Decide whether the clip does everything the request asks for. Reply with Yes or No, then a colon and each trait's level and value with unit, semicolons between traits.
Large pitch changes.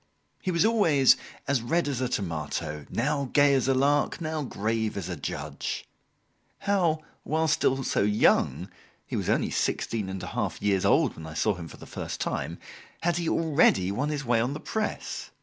Yes: wide, 7.3 semitones